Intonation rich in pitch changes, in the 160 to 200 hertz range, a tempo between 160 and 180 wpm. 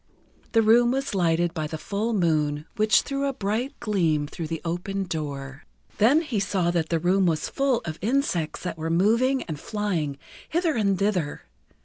Yes: wide, 5.9 semitones; high, 190 Hz; average, 175 wpm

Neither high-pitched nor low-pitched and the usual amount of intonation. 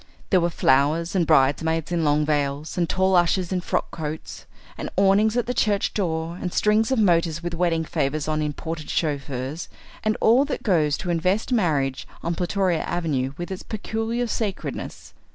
Yes: medium, 170 Hz; average, 4.0 semitones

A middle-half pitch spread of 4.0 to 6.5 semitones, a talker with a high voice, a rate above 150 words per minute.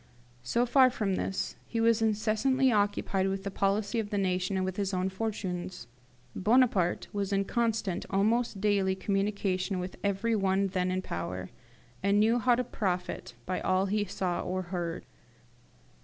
No: average, 2.7 semitones; high, 195 Hz; average, 160 wpm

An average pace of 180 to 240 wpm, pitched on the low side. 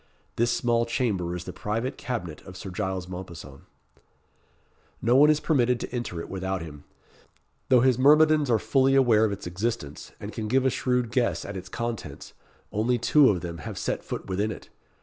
Yes: average, 190 wpm; low, 115 Hz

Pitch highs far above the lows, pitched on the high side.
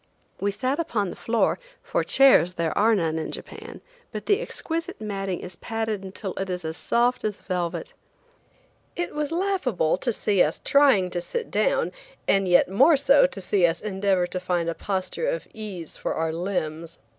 Yes: wide, 6.2 semitones; high, 195 Hz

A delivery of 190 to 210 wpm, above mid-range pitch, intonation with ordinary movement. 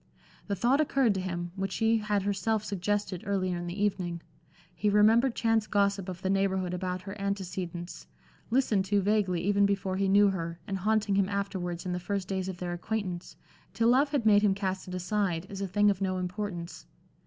No: average, 200 wpm; high, 195 Hz; narrow, 2.3 semitones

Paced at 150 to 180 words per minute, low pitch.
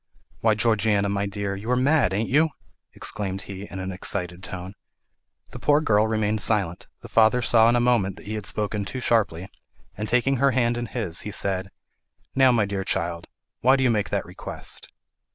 No: average, 190 wpm; low, 105 Hz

